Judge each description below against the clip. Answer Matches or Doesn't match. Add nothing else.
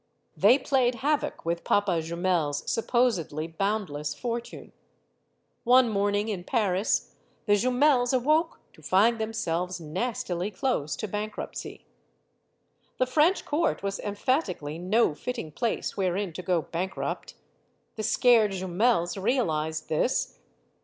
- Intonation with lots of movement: Matches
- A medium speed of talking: Doesn't match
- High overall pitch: Matches